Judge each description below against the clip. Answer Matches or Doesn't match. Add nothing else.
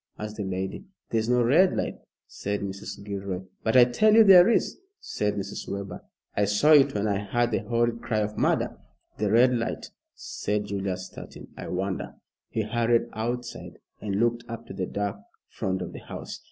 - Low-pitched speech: Matches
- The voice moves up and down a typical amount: Matches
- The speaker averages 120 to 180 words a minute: Doesn't match